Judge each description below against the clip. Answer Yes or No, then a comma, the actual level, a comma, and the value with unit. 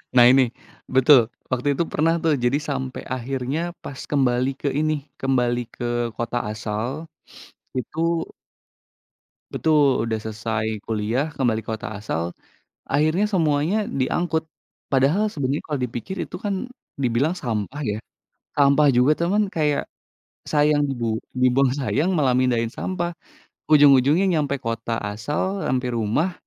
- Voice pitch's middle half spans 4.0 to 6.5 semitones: Yes, average, 4.3 semitones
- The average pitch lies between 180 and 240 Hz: No, low, 135 Hz